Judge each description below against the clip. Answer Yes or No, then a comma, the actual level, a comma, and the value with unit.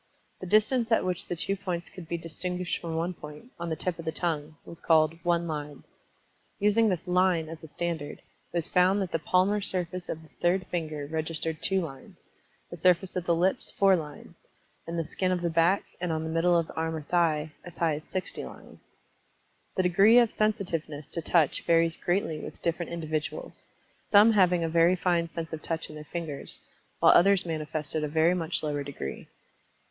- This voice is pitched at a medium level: Yes, medium, 170 Hz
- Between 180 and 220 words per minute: Yes, average, 200 wpm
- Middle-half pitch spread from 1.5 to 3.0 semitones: Yes, narrow, 2.4 semitones